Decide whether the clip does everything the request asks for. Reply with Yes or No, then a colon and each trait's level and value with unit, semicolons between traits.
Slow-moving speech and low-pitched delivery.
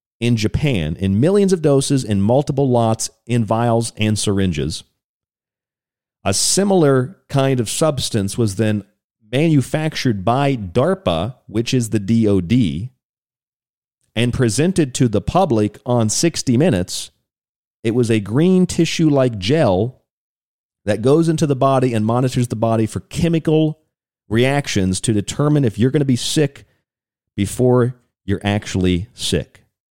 Yes: slow, 130 wpm; low, 120 Hz